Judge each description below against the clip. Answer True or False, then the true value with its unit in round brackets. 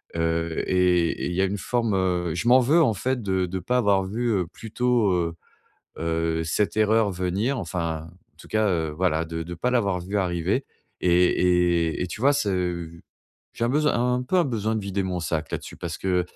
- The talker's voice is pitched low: True (95 Hz)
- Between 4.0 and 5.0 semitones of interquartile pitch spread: True (4.4 semitones)